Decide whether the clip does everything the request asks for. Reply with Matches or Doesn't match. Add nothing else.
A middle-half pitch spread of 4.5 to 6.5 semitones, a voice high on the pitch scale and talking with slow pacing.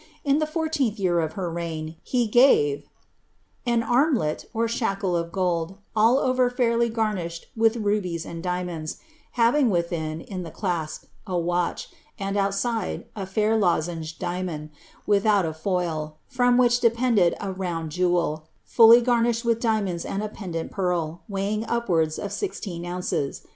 Doesn't match